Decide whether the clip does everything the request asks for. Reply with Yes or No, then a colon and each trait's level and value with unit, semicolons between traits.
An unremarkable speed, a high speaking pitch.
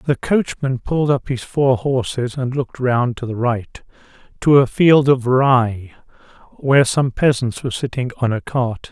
No: average, 175 wpm; low, 130 Hz